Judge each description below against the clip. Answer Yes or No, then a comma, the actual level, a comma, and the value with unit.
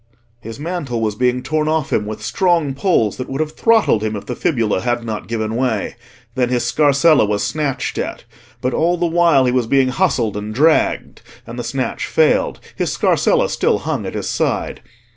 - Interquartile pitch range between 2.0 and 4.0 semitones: No, wide, 5.6 semitones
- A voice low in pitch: Yes, low, 130 Hz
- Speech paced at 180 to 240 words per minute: Yes, average, 190 wpm